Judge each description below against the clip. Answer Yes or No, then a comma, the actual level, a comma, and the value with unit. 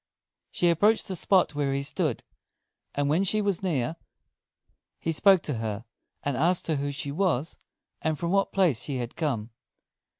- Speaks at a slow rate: No, average, 165 wpm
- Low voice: No, medium, 155 Hz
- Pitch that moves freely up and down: No, average, 4.8 semitones